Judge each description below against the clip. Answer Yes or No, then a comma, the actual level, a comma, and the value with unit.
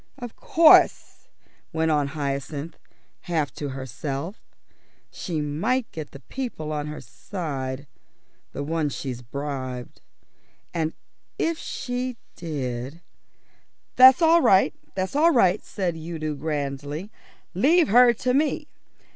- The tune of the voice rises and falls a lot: Yes, wide, 8.3 semitones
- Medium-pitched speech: Yes, medium, 160 Hz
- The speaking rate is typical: No, slow, 120 wpm